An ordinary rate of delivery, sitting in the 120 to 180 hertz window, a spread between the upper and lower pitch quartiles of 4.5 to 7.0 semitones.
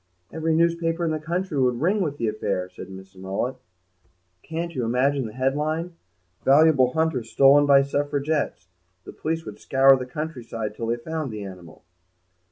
Yes: average, 165 wpm; medium, 140 Hz; wide, 5.4 semitones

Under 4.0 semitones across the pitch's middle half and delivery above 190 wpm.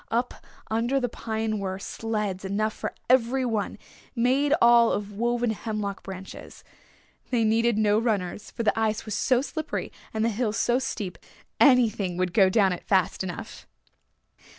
No: average, 2.9 semitones; average, 155 wpm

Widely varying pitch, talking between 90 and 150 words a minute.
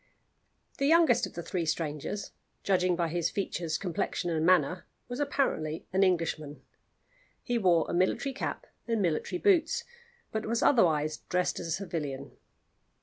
Yes: wide, 6.0 semitones; average, 145 wpm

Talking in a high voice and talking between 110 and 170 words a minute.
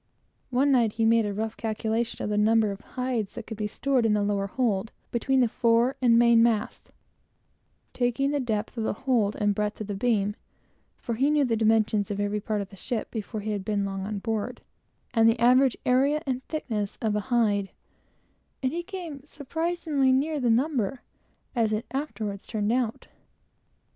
No: high, 225 Hz; average, 190 wpm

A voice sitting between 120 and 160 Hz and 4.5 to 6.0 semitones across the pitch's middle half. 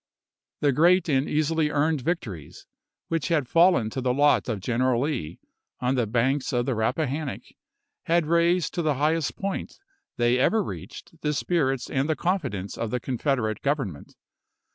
Yes: medium, 140 Hz; average, 4.8 semitones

